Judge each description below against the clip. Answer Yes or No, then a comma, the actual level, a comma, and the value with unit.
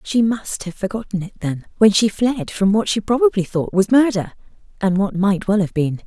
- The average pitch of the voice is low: No, high, 205 Hz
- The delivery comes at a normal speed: No, fast, 220 wpm